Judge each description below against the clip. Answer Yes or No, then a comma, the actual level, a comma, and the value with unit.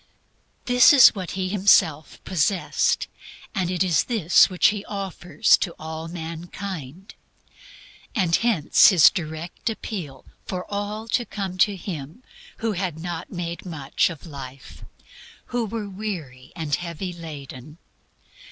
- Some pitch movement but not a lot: Yes, average, 4.0 semitones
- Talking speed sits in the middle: No, slow, 125 wpm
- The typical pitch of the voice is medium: Yes, medium, 180 Hz